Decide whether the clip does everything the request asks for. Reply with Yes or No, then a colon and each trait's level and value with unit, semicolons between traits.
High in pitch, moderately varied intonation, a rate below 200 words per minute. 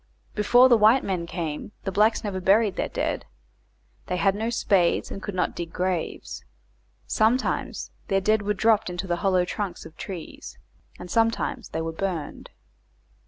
Yes: high, 195 Hz; average, 3.4 semitones; average, 165 wpm